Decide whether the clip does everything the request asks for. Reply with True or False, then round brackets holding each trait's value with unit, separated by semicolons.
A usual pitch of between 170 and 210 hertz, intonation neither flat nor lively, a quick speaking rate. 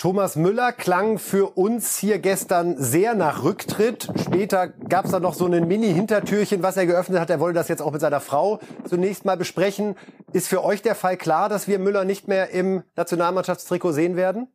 False (185 Hz; 2.2 semitones; 200 wpm)